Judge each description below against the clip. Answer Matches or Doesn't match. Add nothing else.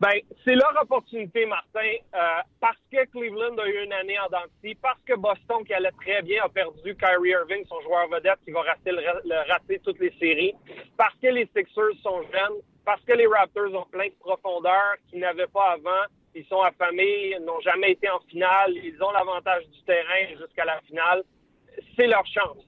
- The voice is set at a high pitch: Matches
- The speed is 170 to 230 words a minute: Matches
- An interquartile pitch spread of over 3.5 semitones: Matches